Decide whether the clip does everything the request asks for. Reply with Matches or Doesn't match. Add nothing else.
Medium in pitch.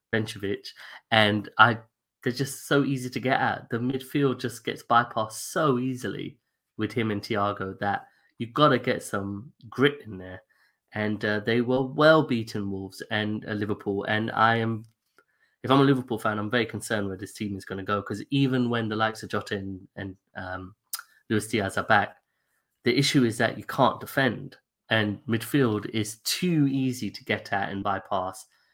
Doesn't match